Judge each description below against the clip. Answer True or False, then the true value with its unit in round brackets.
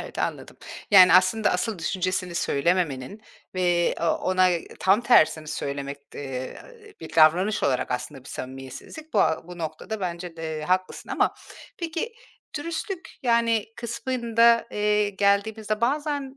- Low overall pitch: False (185 Hz)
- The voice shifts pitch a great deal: True (6.1 semitones)